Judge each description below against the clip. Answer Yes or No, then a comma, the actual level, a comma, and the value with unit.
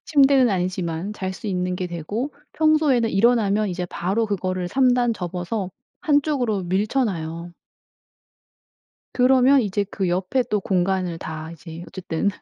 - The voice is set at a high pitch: Yes, high, 195 Hz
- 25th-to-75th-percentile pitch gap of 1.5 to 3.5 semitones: No, wide, 5.5 semitones